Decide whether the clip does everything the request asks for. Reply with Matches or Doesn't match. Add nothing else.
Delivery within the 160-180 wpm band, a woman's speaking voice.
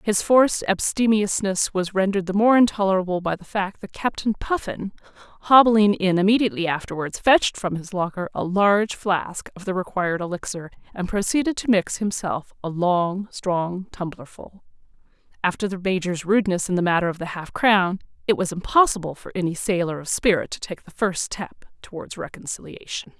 Matches